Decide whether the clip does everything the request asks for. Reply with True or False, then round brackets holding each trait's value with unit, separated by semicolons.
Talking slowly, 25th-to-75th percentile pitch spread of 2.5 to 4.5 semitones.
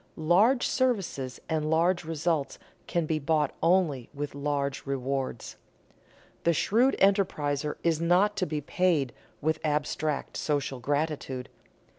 True (120 wpm; 3.6 semitones)